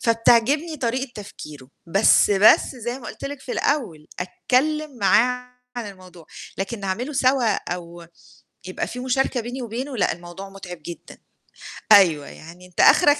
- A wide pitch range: Yes, wide, 5.9 semitones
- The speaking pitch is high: Yes, high, 230 Hz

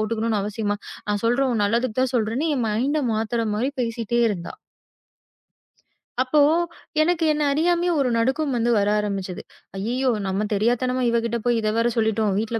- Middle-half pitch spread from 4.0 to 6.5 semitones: No, average, 3.2 semitones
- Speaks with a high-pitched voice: Yes, high, 230 Hz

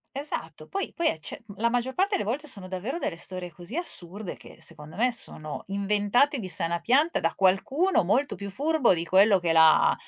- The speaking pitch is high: Yes, high, 205 Hz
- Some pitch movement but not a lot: No, wide, 7.6 semitones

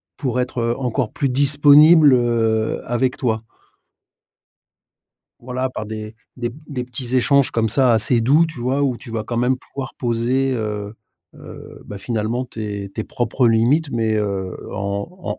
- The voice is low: Yes, low, 120 Hz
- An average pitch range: Yes, average, 3.0 semitones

